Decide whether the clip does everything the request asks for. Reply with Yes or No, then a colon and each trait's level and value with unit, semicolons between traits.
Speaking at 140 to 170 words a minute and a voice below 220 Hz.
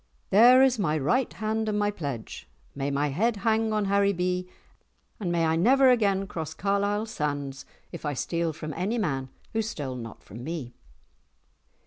Yes: average, 160 wpm; medium, 185 Hz